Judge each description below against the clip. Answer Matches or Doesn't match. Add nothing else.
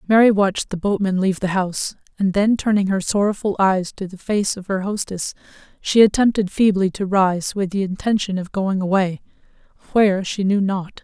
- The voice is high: Matches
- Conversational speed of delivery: Matches